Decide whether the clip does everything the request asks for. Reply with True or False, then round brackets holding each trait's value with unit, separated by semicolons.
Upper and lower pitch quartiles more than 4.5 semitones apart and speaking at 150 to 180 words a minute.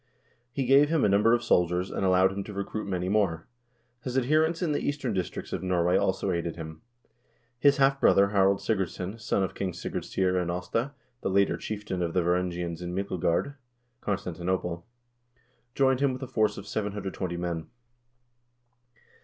True (5.2 semitones; 175 wpm)